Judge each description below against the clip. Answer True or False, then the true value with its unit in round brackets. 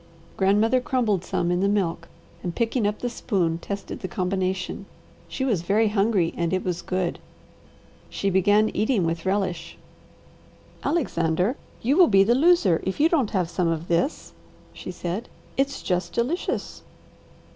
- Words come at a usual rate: True (155 wpm)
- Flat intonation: False (4.6 semitones)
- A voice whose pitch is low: False (195 Hz)